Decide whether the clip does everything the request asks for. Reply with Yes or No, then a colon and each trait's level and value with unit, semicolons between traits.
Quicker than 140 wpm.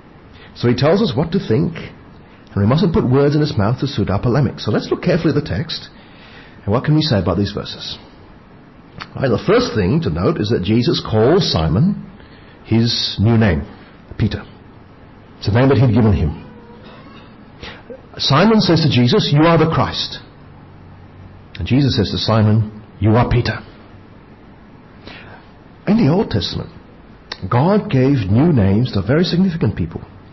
Yes: average, 165 wpm